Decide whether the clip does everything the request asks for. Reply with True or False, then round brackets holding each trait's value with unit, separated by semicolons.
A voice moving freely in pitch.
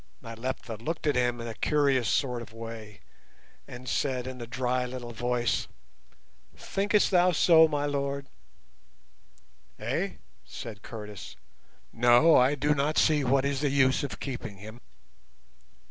False (3.3 semitones)